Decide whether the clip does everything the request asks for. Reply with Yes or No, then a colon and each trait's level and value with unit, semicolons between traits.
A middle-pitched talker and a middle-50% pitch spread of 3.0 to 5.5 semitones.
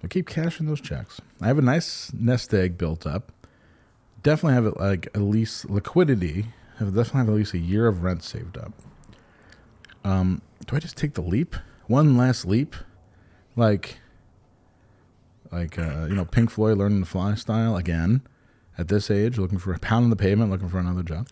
No: low, 105 Hz; average, 4.6 semitones